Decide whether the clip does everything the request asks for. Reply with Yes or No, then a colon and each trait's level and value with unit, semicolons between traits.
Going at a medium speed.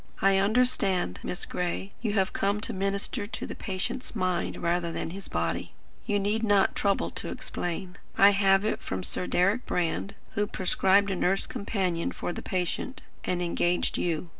Yes: average, 175 wpm